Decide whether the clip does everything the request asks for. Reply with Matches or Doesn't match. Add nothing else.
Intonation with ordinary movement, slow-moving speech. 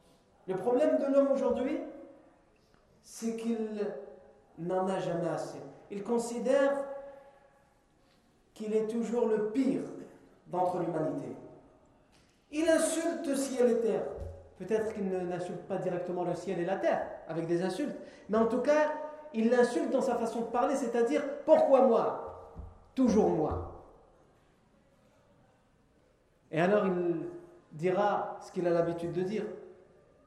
Doesn't match